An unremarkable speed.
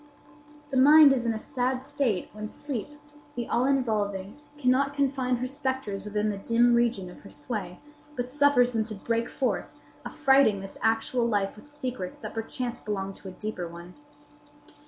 Yes: average, 170 wpm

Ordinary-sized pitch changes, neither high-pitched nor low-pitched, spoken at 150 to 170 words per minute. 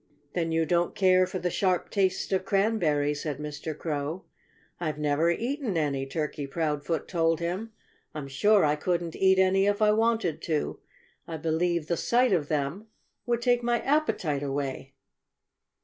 Yes: average, 4.6 semitones; medium, 170 Hz; average, 160 wpm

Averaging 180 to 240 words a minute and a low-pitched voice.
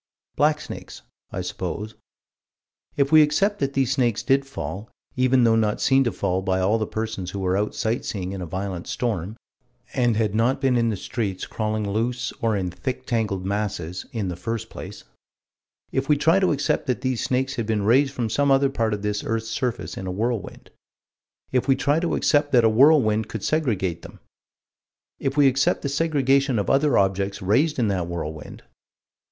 Yes: average, 190 wpm; low, 115 Hz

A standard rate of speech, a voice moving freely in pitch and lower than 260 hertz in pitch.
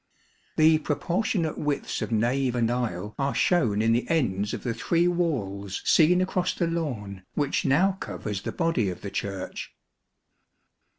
Yes: average, 155 wpm; wide, 7.9 semitones; low, 135 Hz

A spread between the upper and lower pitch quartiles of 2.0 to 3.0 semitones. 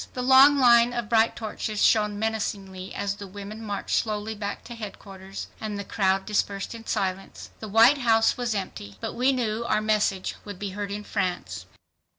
Yes: narrow, 2.4 semitones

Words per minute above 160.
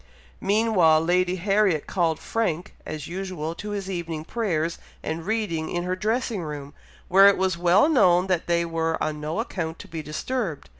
Yes: average, 170 wpm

